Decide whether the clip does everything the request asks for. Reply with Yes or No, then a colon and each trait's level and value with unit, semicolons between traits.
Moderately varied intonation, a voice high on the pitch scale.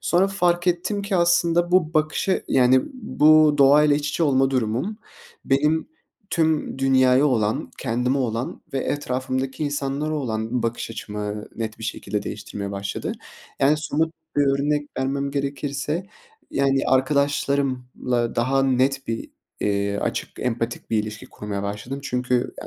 No: average, 4.0 semitones; low, 135 Hz